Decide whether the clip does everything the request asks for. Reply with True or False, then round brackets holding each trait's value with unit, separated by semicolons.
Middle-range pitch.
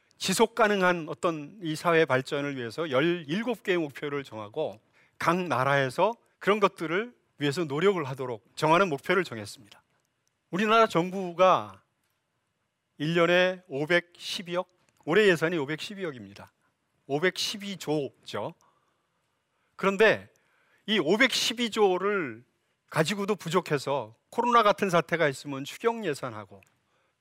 True (170 Hz)